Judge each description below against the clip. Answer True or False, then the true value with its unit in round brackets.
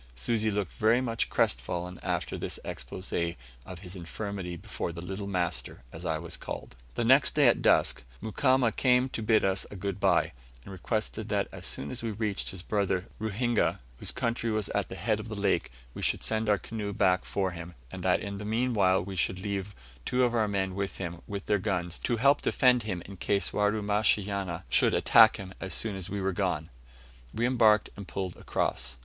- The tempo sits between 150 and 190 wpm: False (200 wpm)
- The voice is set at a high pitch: False (100 Hz)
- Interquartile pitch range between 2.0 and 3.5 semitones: True (3.0 semitones)